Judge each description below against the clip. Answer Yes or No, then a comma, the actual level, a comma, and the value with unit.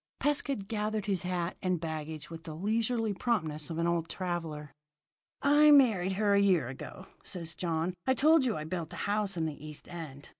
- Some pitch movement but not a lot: Yes, average, 5.0 semitones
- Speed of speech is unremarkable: Yes, average, 190 wpm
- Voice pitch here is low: No, medium, 180 Hz